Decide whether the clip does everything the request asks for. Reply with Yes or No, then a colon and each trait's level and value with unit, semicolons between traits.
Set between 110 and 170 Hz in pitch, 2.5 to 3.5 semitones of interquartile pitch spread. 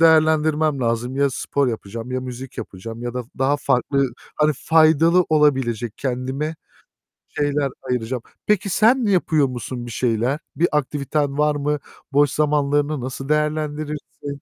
Yes: medium, 140 Hz; average, 3.2 semitones